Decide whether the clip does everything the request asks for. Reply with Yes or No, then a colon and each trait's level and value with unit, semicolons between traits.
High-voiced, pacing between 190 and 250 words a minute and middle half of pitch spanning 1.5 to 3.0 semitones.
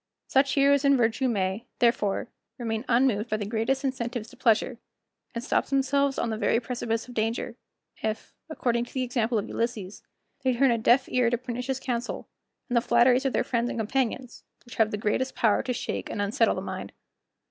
Yes: high, 240 Hz; average, 195 wpm; narrow, 2.5 semitones